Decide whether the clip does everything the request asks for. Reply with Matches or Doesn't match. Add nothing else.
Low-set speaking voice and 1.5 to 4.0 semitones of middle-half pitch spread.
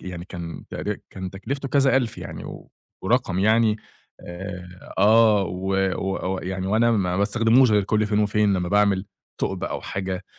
Matches